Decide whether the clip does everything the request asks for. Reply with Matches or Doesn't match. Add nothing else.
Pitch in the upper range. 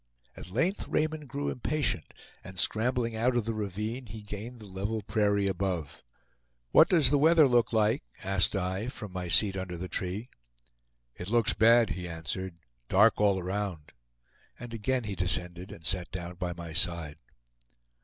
Doesn't match